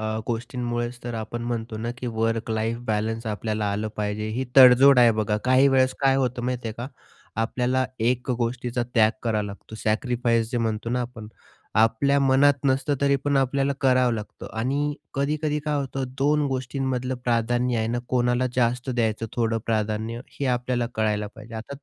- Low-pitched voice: Yes, low, 120 Hz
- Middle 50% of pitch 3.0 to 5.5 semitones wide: No, narrow, 2.6 semitones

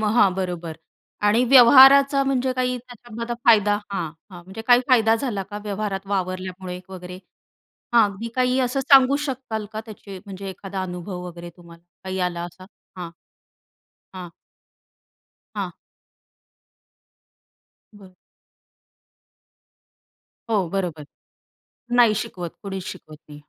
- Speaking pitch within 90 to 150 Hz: No, high, 200 Hz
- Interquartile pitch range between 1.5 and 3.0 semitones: No, average, 4.8 semitones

